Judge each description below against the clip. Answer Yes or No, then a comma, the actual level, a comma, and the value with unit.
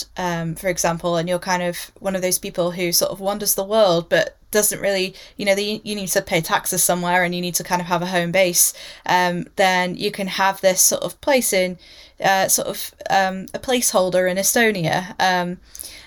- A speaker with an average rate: No, fast, 215 wpm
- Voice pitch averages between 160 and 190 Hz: Yes, medium, 185 Hz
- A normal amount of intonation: No, narrow, 2.0 semitones